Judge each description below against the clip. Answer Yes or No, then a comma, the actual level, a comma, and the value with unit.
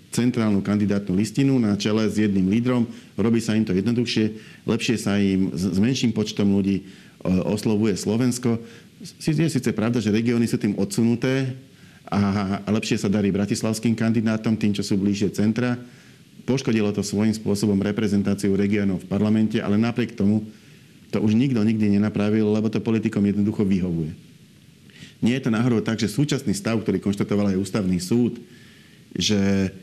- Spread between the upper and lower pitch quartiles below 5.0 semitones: Yes, narrow, 2.5 semitones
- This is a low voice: Yes, low, 110 Hz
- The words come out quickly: No, average, 155 wpm